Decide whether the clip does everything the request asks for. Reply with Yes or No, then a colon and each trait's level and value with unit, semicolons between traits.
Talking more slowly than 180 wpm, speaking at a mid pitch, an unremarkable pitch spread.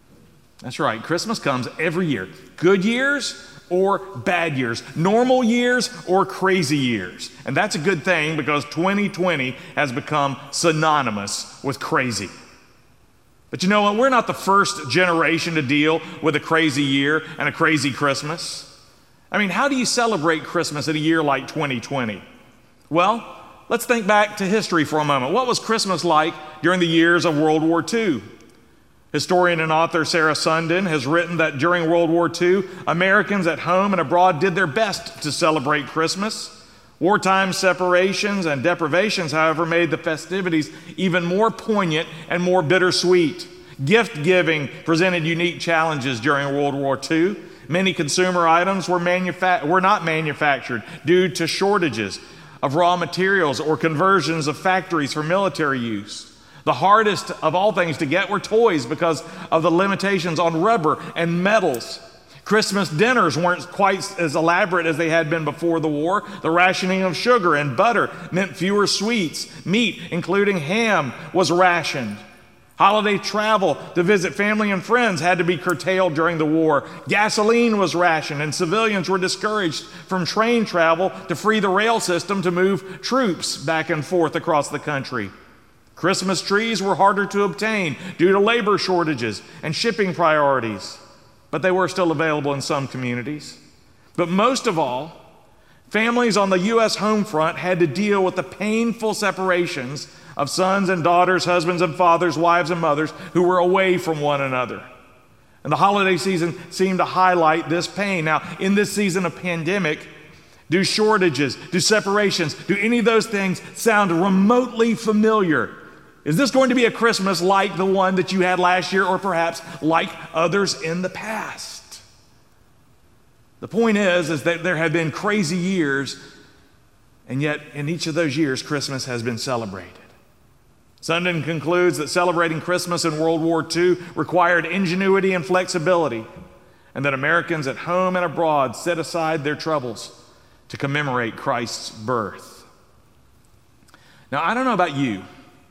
Yes: average, 160 wpm; medium, 175 Hz; average, 3.8 semitones